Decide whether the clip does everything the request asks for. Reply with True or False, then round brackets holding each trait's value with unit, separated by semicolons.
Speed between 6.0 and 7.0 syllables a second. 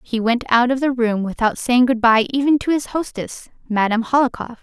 False (5.4 syllables/s)